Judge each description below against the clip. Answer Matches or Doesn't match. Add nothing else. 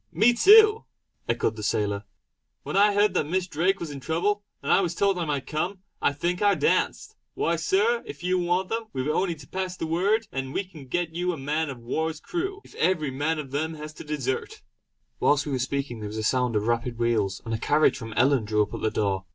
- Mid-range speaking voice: Matches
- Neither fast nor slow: Doesn't match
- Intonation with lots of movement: Matches